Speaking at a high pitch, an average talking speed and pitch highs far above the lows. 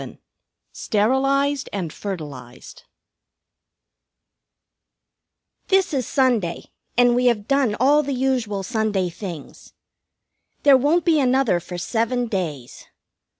No: high, 240 Hz; slow, 105 wpm; wide, 6.1 semitones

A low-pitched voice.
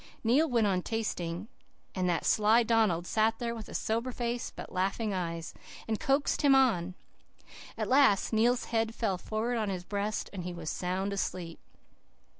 No: high, 215 Hz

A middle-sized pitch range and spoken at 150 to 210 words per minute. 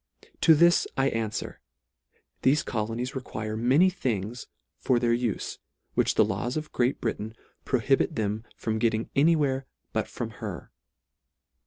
No: average, 3.7 semitones; average, 140 wpm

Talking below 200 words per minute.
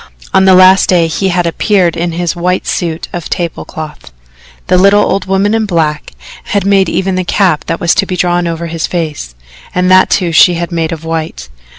No: fast, 205 wpm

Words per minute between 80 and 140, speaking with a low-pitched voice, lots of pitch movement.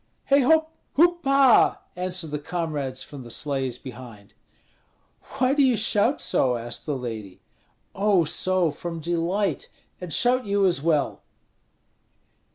No: slow, 135 wpm; medium, 170 Hz; wide, 8.0 semitones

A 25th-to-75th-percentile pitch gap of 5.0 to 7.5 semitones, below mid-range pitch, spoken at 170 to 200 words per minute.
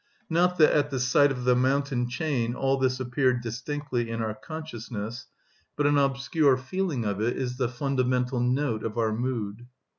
No: average, 2.9 semitones; low, 130 Hz; average, 175 wpm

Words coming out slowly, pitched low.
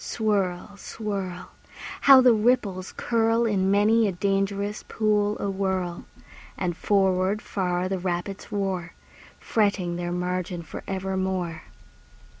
No: slow, 110 wpm; high, 195 Hz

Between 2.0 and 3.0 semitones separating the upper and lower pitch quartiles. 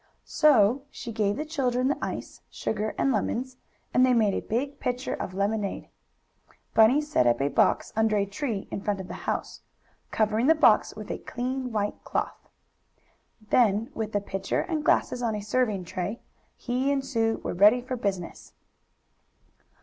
No: average, 3.8 semitones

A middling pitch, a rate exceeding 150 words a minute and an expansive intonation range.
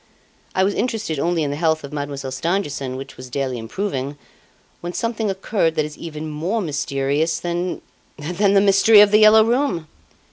Yes: medium, 165 Hz; average, 175 wpm; wide, 5.9 semitones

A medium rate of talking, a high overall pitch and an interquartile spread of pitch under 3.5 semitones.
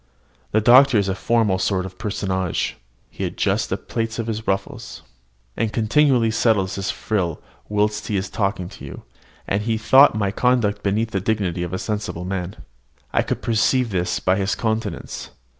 No: average, 175 wpm; low, 105 Hz; average, 2.9 semitones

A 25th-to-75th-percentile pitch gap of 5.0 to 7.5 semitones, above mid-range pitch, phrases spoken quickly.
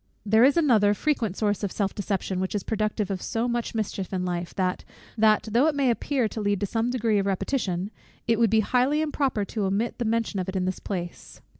No: average, 3.4 semitones; high, 215 Hz; fast, 225 wpm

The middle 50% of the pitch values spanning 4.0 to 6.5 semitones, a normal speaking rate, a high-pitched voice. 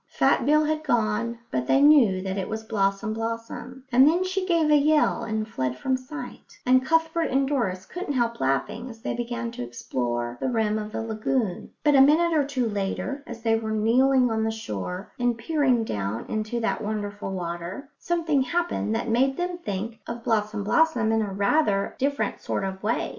Yes: average, 5.0 semitones; average, 195 wpm; high, 230 Hz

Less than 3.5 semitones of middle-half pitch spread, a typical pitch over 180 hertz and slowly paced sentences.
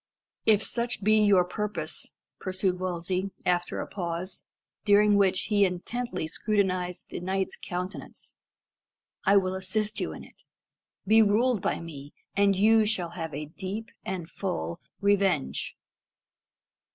Yes: narrow, 2.6 semitones; high, 190 Hz; slow, 130 wpm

